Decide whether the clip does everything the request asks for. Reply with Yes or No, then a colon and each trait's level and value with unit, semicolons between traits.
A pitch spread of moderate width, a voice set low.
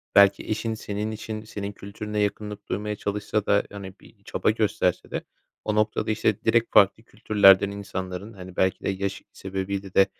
No: narrow, 1.6 semitones; low, 100 Hz